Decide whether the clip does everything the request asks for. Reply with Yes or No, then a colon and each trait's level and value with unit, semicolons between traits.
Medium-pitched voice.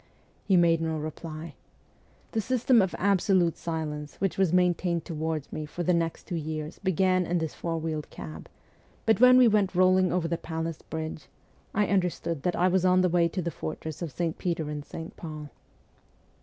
Yes: medium, 170 Hz